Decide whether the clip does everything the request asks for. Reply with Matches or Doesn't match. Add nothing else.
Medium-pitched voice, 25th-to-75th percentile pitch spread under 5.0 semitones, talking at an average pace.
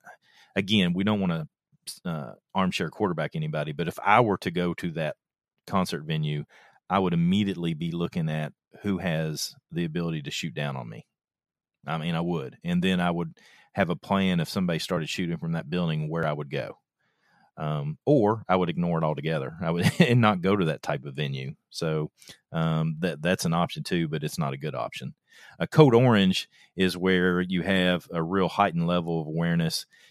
Doesn't match